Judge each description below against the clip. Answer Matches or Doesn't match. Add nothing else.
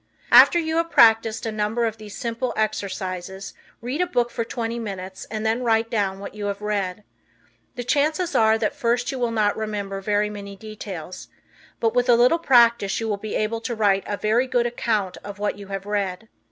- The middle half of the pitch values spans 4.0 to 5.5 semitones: Doesn't match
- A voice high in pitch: Matches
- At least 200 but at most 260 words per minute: Matches